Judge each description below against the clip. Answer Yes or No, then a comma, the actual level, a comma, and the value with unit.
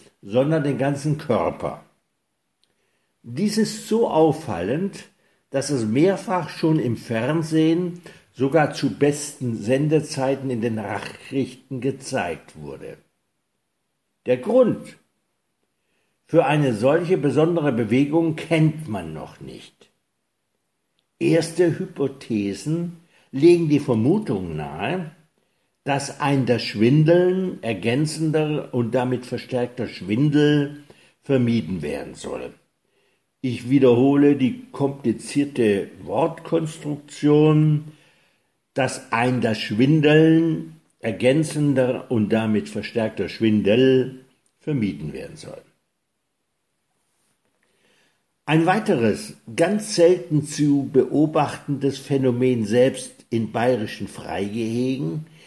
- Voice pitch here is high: No, medium, 140 Hz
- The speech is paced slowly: Yes, slow, 85 wpm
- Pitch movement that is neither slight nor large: Yes, average, 4.5 semitones